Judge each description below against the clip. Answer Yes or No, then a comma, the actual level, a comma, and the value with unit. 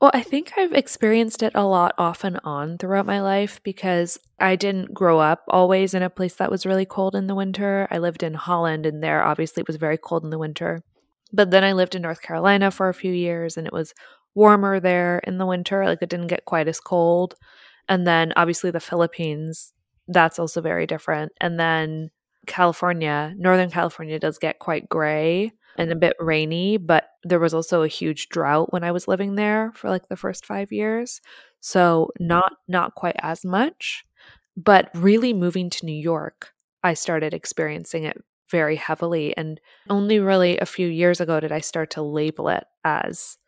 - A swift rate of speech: No, average, 195 wpm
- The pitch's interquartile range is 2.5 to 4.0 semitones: Yes, average, 3.0 semitones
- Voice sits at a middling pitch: Yes, medium, 175 Hz